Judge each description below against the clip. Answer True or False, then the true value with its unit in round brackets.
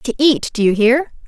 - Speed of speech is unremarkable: True (190 wpm)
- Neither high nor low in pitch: False (250 Hz)